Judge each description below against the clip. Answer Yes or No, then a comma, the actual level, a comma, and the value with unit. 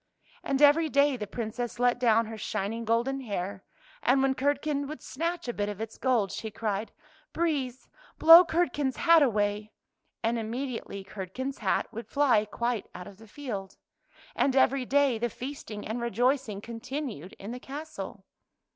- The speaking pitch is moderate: No, high, 240 Hz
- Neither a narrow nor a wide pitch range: Yes, average, 4.5 semitones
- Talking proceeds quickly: No, average, 165 wpm